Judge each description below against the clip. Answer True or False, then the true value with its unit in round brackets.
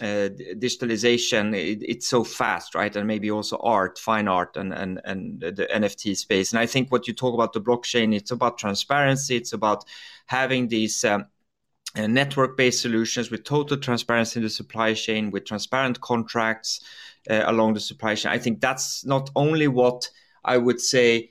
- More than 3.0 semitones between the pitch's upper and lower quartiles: False (2.5 semitones)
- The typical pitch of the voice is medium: False (115 Hz)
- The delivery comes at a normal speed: True (175 wpm)